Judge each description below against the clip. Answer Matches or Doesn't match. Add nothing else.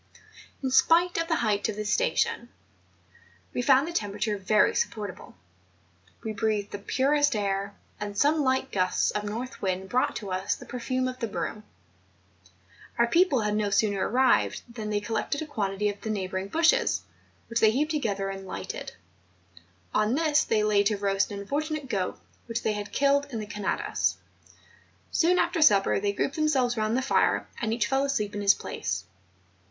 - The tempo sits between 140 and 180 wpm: Matches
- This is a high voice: Matches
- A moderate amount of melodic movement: Matches